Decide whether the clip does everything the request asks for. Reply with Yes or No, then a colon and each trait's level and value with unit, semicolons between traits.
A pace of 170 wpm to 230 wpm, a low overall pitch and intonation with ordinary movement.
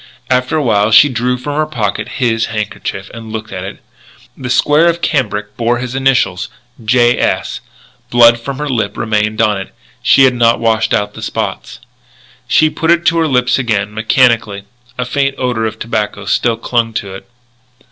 Yes: average, 180 wpm; low, 120 Hz; average, 3.2 semitones